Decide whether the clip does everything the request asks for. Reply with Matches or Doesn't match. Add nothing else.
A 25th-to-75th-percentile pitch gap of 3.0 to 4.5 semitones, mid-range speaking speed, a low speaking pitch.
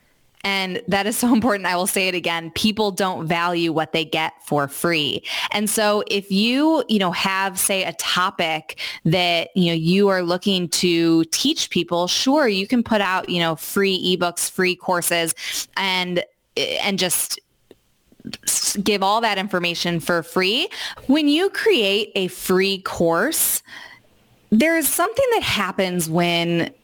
Doesn't match